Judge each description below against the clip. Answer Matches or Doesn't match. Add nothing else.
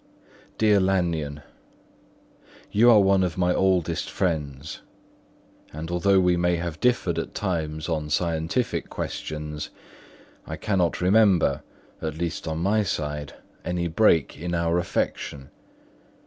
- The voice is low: Matches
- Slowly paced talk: Matches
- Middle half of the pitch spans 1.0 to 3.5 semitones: Matches